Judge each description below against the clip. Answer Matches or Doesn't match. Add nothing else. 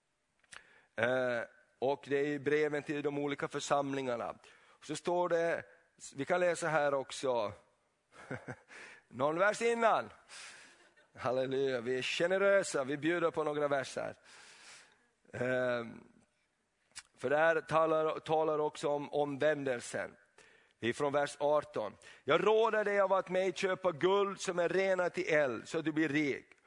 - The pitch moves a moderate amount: Matches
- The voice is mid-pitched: Matches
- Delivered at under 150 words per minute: Matches